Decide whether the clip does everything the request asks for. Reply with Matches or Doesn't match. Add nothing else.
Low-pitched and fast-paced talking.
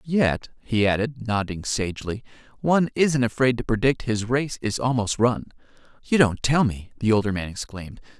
Doesn't match